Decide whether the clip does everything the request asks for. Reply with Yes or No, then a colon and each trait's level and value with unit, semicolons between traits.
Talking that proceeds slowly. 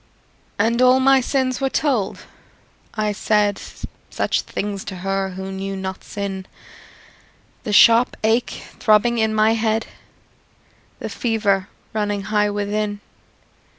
Yes: slow, 120 wpm